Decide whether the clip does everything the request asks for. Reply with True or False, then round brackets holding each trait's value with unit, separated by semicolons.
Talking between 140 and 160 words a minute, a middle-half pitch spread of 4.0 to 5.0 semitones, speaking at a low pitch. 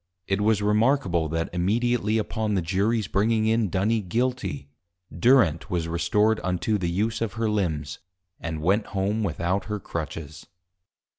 True (145 wpm; 4.4 semitones; 100 Hz)